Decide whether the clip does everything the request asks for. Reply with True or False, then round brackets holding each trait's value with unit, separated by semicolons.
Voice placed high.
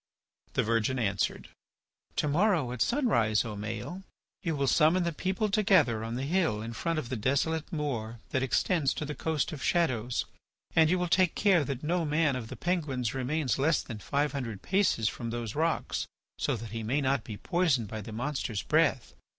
False (140 Hz)